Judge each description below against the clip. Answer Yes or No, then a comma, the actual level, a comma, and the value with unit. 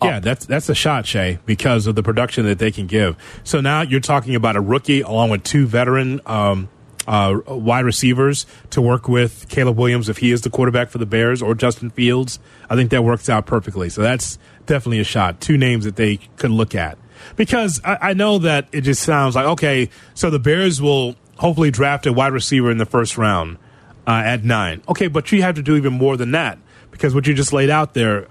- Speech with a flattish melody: No, average, 4.2 semitones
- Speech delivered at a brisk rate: Yes, fast, 225 wpm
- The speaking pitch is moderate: No, low, 125 Hz